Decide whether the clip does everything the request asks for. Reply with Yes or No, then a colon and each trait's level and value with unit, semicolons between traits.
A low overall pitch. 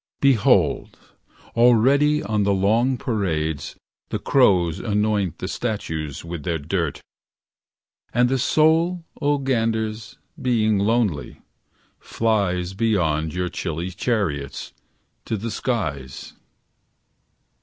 Yes: low, 105 Hz